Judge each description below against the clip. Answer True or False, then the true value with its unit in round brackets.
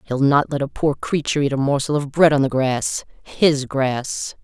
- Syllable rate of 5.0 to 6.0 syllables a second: False (4.6 syllables/s)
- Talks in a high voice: False (140 Hz)